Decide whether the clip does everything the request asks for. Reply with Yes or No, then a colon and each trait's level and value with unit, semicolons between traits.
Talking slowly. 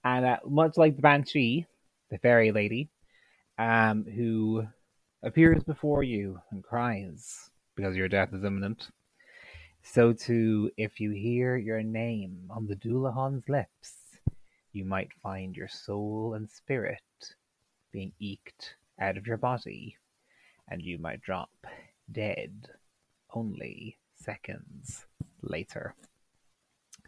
Yes: slow, 115 wpm